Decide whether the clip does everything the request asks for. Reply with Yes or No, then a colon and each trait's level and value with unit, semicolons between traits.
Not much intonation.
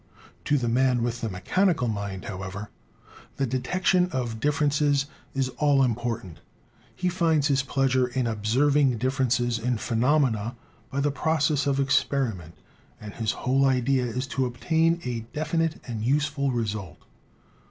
No: average, 3.7 semitones